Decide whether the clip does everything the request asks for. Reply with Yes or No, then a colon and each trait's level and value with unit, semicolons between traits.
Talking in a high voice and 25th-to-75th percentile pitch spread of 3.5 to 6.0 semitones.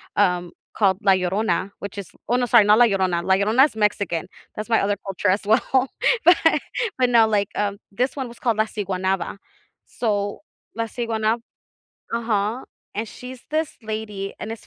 No: high, 215 Hz; average, 2.8 semitones